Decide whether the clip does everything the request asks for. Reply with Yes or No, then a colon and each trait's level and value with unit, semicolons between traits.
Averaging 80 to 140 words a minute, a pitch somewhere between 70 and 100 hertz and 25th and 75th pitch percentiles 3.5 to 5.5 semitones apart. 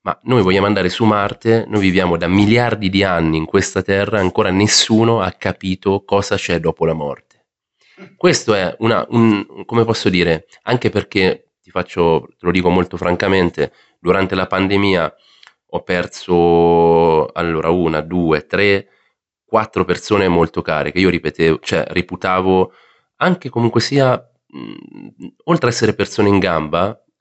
No: average, 150 wpm; very low, 95 Hz; average, 3.9 semitones